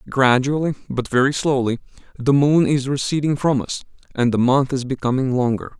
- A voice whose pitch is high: No, low, 135 Hz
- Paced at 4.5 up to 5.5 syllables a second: Yes, 5.3 syllables/s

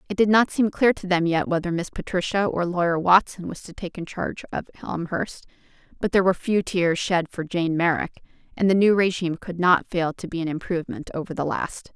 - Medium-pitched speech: Yes, medium, 180 Hz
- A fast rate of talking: Yes, fast, 215 wpm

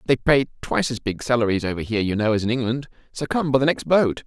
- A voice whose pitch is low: Yes, low, 125 Hz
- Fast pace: Yes, fast, 270 wpm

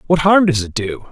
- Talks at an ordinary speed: No, fast, 270 wpm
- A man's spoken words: Yes, male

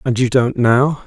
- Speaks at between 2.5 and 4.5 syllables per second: Yes, 4.1 syllables/s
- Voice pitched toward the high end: No, low, 125 Hz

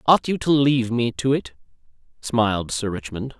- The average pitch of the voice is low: Yes, low, 120 Hz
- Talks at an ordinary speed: Yes, average, 175 wpm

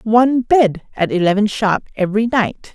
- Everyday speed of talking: Yes, average, 155 wpm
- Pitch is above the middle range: Yes, high, 215 Hz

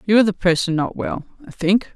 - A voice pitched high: Yes, high, 195 Hz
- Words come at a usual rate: No, fast, 245 wpm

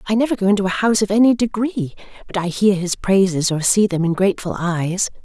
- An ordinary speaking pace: No, fast, 230 wpm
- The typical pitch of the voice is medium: No, high, 195 Hz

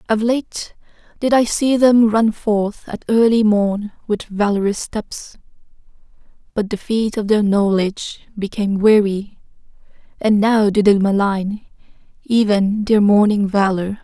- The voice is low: No, high, 210 Hz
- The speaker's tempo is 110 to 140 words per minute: Yes, slow, 135 wpm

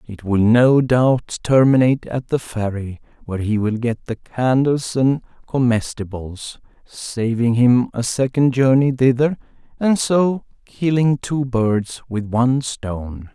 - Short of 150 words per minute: Yes, slow, 135 wpm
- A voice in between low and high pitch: No, low, 125 Hz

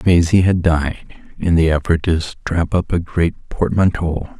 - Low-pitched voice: Yes, very low, 85 Hz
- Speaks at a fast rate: No, average, 165 wpm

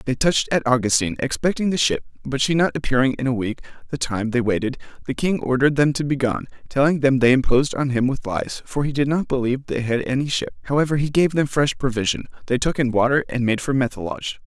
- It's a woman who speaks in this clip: No, male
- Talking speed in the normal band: No, fast, 230 wpm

